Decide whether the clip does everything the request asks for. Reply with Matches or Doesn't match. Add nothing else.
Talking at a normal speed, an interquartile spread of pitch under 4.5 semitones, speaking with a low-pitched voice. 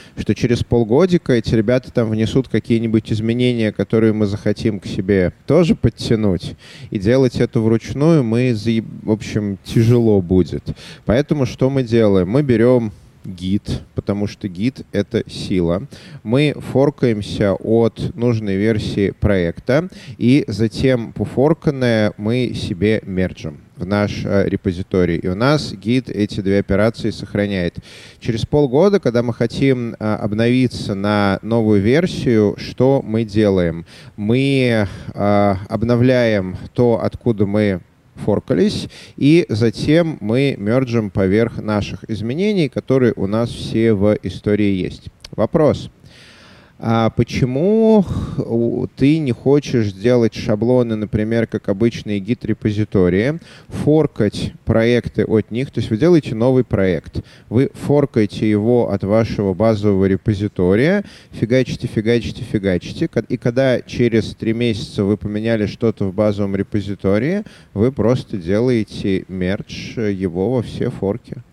Matches